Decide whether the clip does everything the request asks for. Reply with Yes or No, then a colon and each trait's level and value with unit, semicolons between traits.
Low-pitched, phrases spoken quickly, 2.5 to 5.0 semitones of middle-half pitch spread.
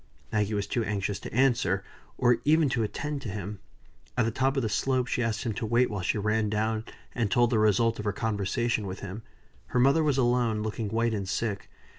Yes: low, 110 Hz; fast, 220 wpm; average, 2.9 semitones